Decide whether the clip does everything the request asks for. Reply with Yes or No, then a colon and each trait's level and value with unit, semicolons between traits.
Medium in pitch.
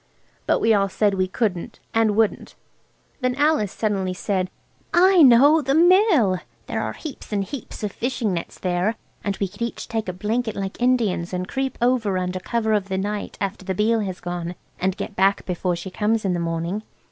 No: high, 205 Hz